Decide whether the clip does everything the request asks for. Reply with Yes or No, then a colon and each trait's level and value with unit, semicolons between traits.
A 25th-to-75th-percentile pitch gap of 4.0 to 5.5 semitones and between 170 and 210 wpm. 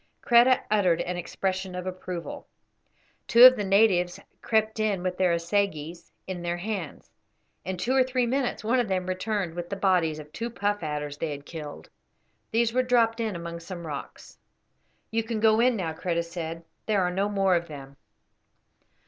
Yes: average, 4.4 semitones; average, 180 wpm